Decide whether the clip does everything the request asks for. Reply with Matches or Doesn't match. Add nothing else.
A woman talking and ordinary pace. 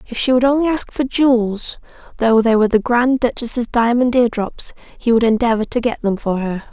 Matches